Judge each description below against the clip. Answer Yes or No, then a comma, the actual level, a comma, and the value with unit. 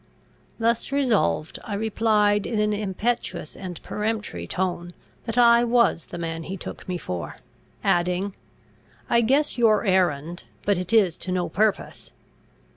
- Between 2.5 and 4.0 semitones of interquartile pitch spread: No, average, 4.4 semitones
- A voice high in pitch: Yes, high, 200 Hz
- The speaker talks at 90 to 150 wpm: Yes, average, 140 wpm